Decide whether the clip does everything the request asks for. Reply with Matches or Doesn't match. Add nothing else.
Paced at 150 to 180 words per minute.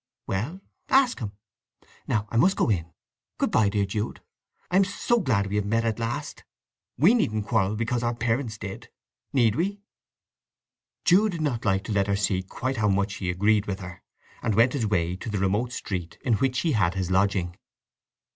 Doesn't match